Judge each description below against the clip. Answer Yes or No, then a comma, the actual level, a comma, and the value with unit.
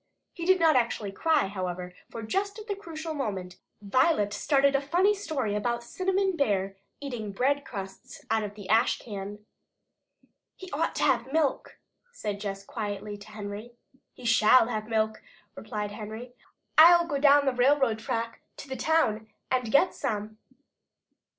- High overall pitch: Yes, high, 235 Hz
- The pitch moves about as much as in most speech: No, wide, 5.7 semitones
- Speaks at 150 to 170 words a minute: Yes, average, 155 wpm